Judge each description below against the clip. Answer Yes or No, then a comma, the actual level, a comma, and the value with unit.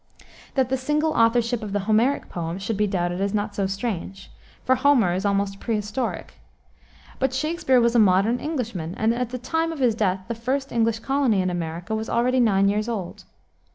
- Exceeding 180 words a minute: Yes, average, 190 wpm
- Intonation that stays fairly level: No, average, 4.3 semitones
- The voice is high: Yes, high, 225 Hz